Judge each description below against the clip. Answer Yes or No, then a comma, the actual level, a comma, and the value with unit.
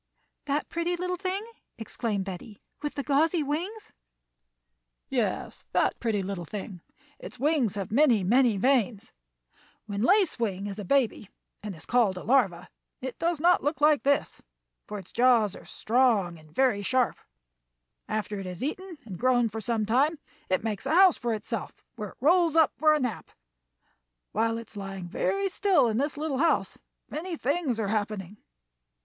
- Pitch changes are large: Yes, wide, 6.7 semitones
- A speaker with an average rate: Yes, average, 170 wpm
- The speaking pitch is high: Yes, high, 240 Hz